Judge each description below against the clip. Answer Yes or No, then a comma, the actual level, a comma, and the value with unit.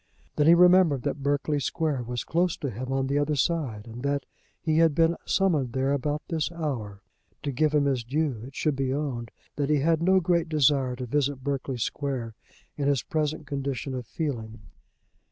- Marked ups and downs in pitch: No, average, 3.1 semitones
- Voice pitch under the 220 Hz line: Yes, medium, 140 Hz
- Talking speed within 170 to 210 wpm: Yes, average, 190 wpm